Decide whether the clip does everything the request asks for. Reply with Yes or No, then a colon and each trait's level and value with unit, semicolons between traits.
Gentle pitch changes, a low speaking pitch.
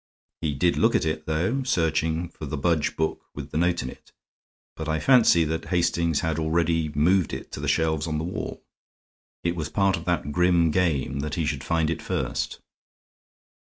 Yes: narrow, 1.9 semitones; very low, 80 Hz